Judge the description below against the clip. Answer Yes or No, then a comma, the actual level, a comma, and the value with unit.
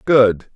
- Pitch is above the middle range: No, low, 115 Hz